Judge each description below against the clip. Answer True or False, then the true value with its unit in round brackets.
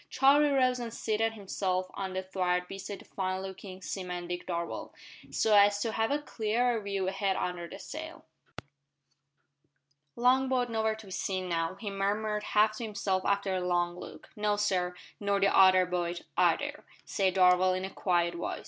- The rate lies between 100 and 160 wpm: False (175 wpm)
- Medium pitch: False (195 Hz)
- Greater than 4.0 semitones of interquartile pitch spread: False (2.9 semitones)